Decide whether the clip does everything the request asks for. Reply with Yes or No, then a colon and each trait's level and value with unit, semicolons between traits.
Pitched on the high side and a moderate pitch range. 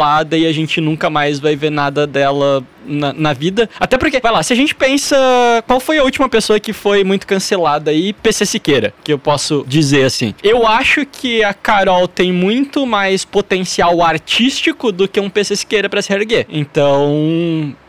No: high, 195 Hz; wide, 6.8 semitones